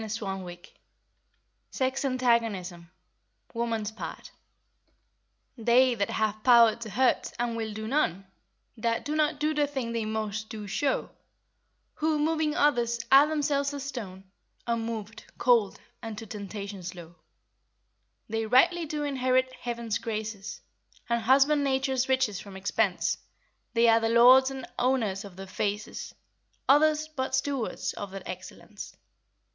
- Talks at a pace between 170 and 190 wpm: No, slow, 135 wpm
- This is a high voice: Yes, high, 235 Hz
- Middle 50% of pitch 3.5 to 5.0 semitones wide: Yes, average, 4.0 semitones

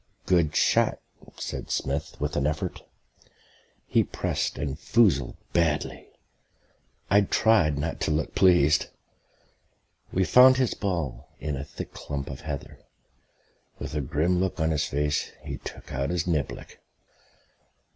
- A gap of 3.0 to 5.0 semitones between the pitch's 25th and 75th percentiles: Yes, average, 3.8 semitones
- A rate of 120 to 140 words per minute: Yes, slow, 135 wpm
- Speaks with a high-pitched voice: No, very low, 75 Hz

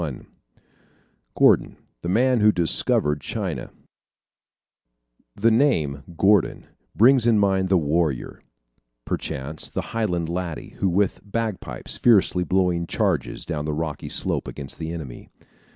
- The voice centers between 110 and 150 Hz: No, very low, 90 Hz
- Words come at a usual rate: No, slow, 120 wpm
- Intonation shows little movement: No, average, 5.0 semitones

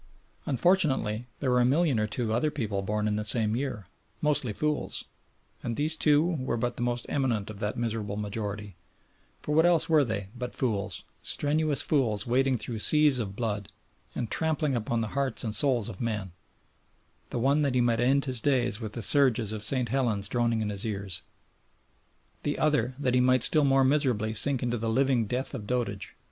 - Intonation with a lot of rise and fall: No, average, 4.2 semitones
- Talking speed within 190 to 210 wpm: Yes, average, 195 wpm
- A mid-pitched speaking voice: No, low, 120 Hz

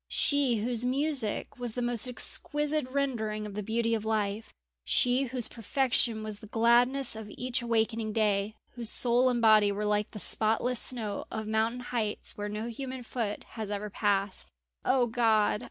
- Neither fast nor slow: Yes, average, 170 wpm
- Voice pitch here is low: No, high, 225 Hz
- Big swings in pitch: No, average, 2.7 semitones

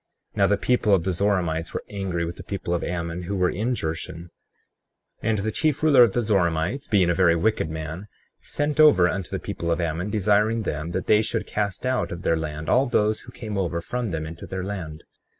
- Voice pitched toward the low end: Yes, very low, 95 Hz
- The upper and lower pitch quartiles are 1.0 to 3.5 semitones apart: No, average, 4.3 semitones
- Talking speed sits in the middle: No, fast, 220 wpm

